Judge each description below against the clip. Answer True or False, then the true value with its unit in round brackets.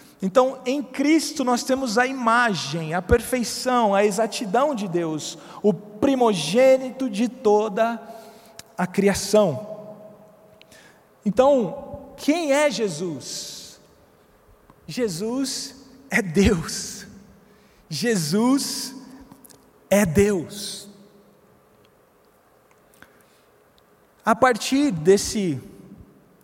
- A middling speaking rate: False (75 wpm)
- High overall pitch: True (225 Hz)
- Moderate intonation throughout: True (4.2 semitones)